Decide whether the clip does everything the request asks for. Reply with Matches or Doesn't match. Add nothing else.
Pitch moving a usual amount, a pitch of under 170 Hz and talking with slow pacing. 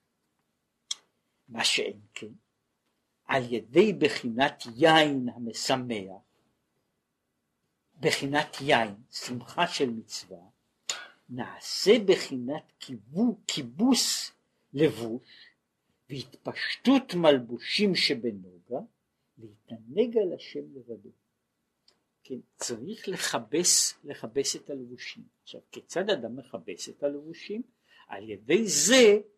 Doesn't match